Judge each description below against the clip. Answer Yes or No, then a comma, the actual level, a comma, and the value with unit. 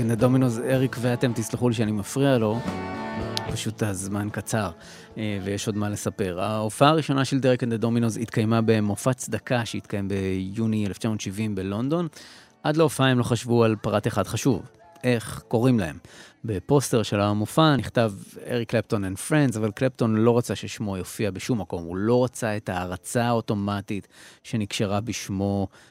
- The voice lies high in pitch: No, low, 115 Hz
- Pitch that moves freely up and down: No, average, 3.0 semitones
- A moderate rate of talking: No, fast, 155 wpm